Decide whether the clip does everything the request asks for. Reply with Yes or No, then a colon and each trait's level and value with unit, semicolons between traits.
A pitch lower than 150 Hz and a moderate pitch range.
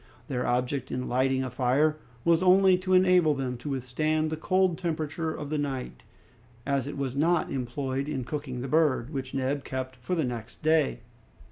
Yes: medium, 140 Hz; average, 3.5 semitones